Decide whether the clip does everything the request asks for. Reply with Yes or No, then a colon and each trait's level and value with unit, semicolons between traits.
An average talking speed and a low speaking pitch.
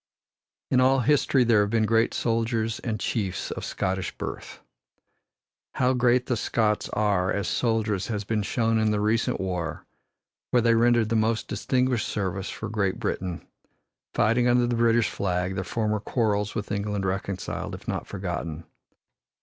Yes: average, 155 wpm; low, 110 Hz